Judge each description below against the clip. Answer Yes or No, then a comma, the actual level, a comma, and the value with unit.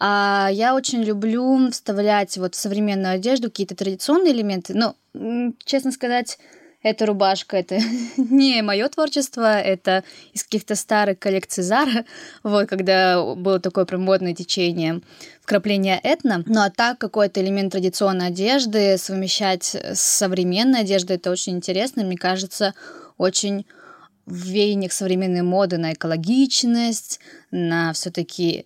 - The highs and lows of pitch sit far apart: No, average, 3.8 semitones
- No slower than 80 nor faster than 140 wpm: Yes, average, 125 wpm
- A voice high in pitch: Yes, high, 200 Hz